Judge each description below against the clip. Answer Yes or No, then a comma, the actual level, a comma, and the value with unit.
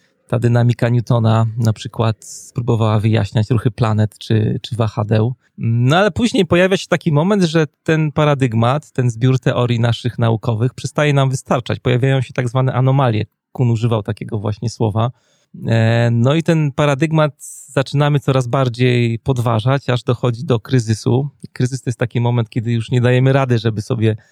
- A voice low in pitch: Yes, low, 125 Hz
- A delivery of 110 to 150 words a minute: No, fast, 160 wpm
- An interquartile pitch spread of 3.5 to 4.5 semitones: No, average, 2.9 semitones